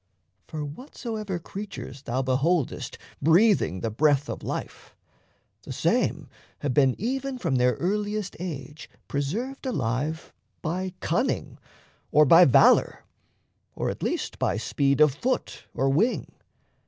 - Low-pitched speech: No, medium, 155 Hz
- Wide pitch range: Yes, wide, 7.2 semitones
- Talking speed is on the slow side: Yes, slow, 125 wpm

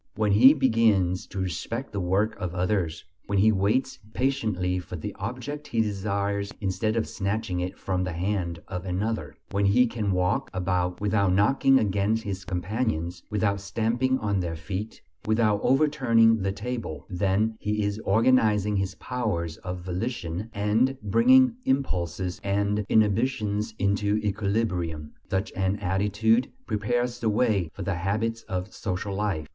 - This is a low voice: Yes, low, 105 Hz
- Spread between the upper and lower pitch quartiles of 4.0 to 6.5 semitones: No, average, 3.2 semitones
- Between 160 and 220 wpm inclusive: No, average, 150 wpm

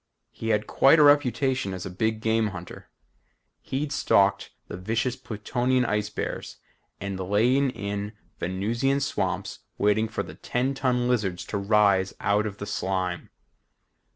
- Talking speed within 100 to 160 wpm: Yes, average, 145 wpm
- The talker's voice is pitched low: Yes, low, 110 Hz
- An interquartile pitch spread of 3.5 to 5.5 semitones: Yes, average, 4.0 semitones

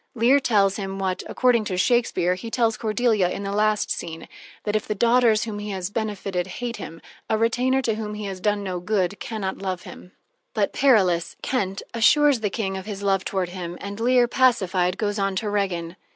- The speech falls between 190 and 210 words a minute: Yes, fast, 205 wpm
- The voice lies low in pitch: No, high, 205 Hz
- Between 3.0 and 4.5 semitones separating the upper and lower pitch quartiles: Yes, average, 3.3 semitones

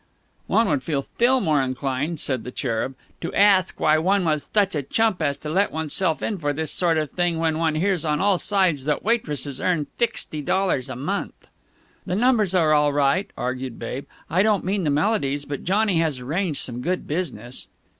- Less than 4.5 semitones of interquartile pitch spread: No, average, 5.1 semitones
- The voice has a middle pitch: Yes, medium, 160 Hz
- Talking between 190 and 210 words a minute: Yes, average, 195 wpm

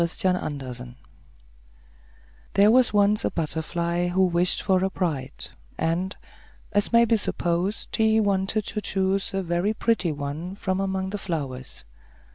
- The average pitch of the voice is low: No, medium, 185 Hz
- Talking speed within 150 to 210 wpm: No, average, 140 wpm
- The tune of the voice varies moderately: Yes, average, 3.2 semitones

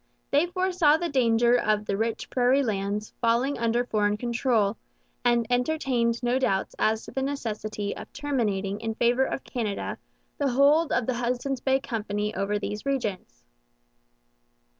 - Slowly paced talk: No, average, 150 wpm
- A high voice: Yes, high, 240 Hz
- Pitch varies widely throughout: No, average, 4.0 semitones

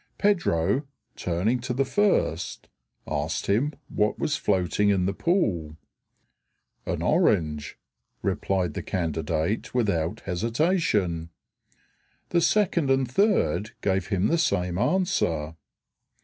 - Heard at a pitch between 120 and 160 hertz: No, low, 100 Hz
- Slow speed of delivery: Yes, slow, 105 wpm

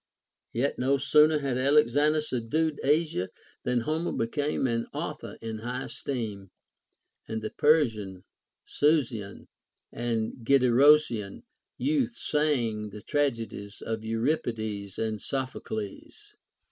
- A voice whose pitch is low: Yes, low, 125 Hz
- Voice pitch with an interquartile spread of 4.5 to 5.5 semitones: Yes, average, 5.1 semitones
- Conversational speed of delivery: No, slow, 110 wpm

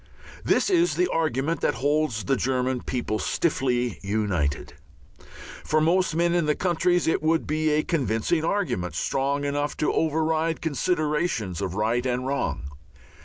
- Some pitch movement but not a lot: Yes, average, 5.0 semitones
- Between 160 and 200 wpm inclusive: No, average, 145 wpm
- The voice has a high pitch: No, medium, 145 Hz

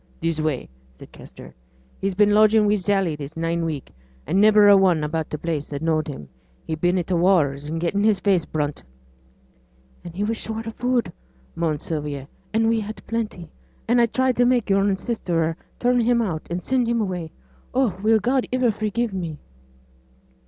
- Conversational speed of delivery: Yes, average, 190 wpm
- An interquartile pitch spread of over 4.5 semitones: Yes, wide, 5.5 semitones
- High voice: Yes, high, 195 Hz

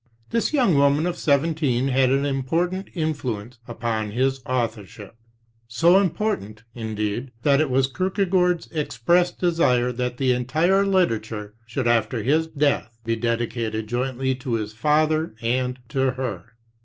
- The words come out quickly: No, average, 140 wpm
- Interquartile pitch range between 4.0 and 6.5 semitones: Yes, average, 5.3 semitones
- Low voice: Yes, low, 130 Hz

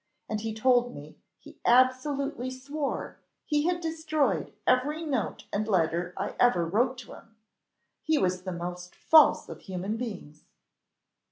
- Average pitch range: No, wide, 7.4 semitones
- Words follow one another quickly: No, average, 145 wpm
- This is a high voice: Yes, high, 245 Hz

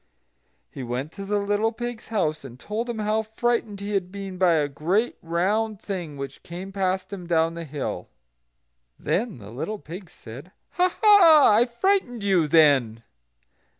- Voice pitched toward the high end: Yes, high, 195 Hz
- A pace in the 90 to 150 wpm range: No, average, 165 wpm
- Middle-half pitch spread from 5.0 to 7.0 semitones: Yes, average, 5.3 semitones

